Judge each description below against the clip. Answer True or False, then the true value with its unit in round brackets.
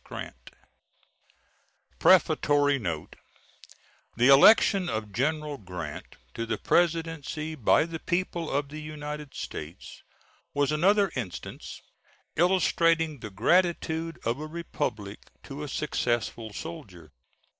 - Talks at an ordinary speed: False (105 wpm)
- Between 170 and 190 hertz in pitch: False (150 Hz)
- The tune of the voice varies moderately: False (6.1 semitones)